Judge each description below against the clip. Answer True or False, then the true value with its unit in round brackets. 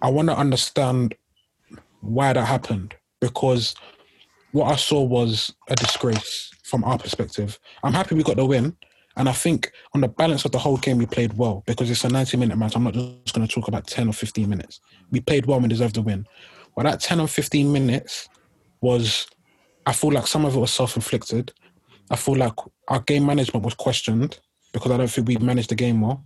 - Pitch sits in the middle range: False (125 Hz)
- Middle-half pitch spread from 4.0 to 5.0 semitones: False (2.9 semitones)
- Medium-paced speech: False (215 wpm)